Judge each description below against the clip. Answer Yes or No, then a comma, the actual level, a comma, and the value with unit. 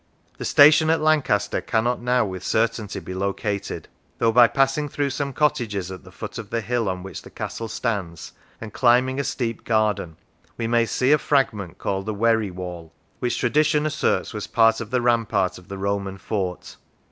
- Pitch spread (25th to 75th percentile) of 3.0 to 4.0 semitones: No, average, 4.4 semitones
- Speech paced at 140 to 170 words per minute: No, average, 185 wpm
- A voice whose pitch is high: No, low, 115 Hz